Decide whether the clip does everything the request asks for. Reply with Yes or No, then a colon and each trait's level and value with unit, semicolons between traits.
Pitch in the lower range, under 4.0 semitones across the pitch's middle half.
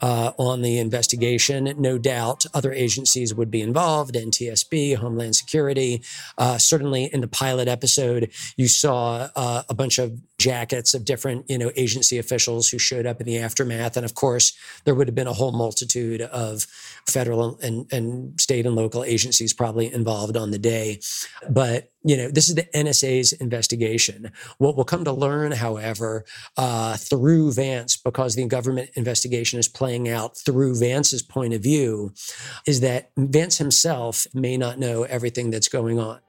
Yes: low, 125 Hz; narrow, 2.4 semitones